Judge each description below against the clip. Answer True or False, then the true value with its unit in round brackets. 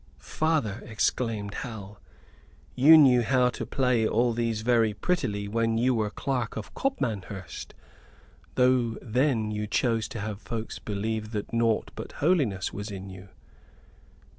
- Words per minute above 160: False (140 wpm)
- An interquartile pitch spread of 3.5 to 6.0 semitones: False (3.1 semitones)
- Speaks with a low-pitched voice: True (115 Hz)